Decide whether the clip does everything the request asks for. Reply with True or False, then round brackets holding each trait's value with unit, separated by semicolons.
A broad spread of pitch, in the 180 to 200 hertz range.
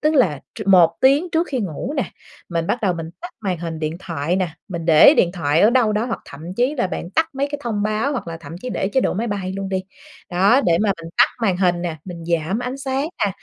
True (6.5 semitones; 190 Hz)